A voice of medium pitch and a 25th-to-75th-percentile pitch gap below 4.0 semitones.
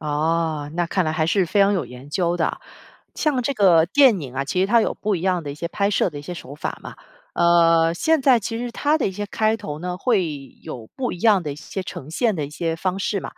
No: medium, 180 Hz; average, 4.5 semitones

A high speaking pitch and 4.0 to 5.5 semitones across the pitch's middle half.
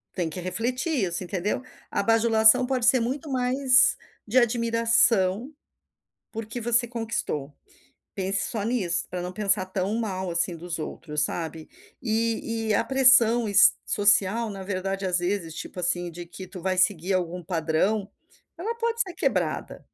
Yes: high, 205 Hz; average, 4.5 semitones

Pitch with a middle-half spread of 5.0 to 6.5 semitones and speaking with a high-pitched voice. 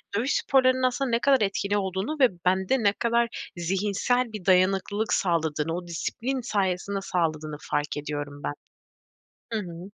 Yes: wide, 5.4 semitones; high, 195 Hz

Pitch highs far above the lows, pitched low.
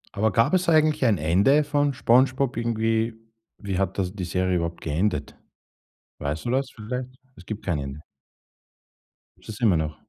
Yes: wide, 6.2 semitones; low, 110 Hz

